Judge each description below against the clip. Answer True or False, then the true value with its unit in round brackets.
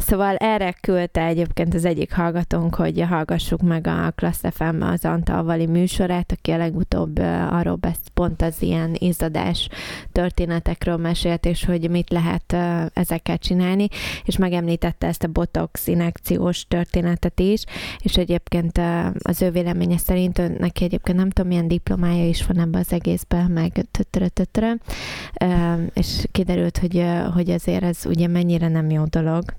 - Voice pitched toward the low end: False (175 Hz)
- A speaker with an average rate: True (140 wpm)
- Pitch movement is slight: True (1.2 semitones)